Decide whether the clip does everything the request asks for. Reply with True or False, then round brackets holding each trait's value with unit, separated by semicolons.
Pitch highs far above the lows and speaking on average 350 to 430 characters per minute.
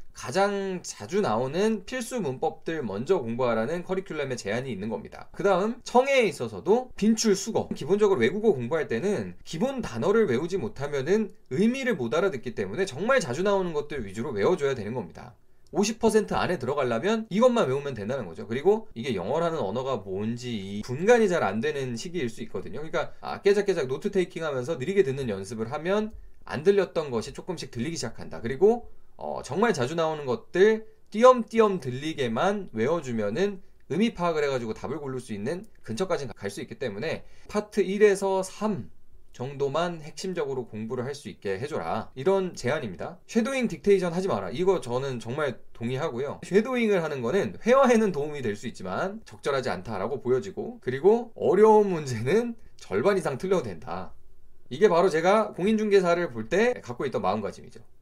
True (8.1 semitones; 385 characters per minute)